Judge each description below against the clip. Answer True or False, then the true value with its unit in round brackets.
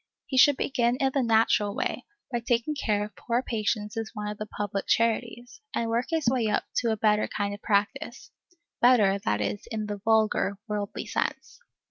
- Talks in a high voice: True (220 Hz)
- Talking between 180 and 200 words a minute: True (190 wpm)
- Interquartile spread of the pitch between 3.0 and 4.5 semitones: False (2.6 semitones)